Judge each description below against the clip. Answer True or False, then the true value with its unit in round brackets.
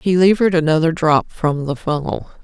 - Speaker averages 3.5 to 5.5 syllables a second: True (5.2 syllables/s)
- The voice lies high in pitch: False (165 Hz)